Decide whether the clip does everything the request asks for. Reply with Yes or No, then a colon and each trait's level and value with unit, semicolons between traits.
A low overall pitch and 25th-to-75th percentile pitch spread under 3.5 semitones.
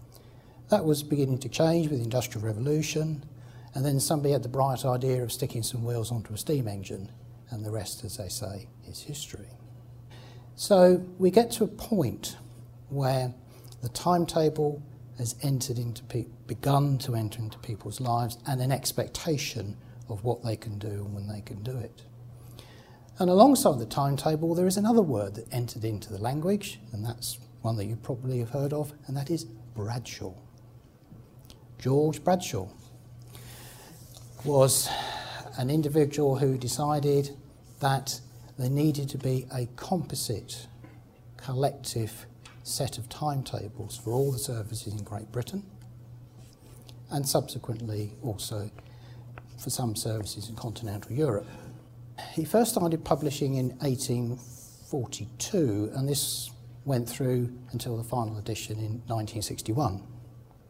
Yes: low, 125 Hz; average, 3.0 semitones